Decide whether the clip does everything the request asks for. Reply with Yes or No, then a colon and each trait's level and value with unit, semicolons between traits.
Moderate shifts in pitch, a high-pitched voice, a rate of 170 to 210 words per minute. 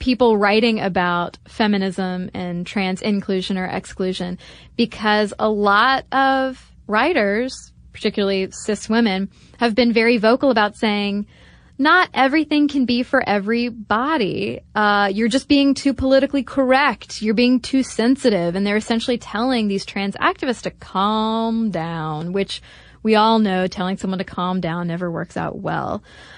No: average, 4.3 semitones; high, 215 Hz; average, 145 wpm